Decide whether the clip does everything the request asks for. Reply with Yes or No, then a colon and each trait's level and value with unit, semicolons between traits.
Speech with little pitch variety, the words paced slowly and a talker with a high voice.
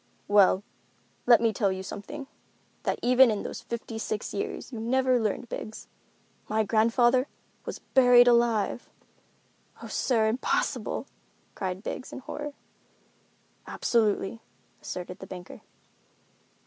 No: average, 3.2 semitones; slow, 120 wpm; high, 225 Hz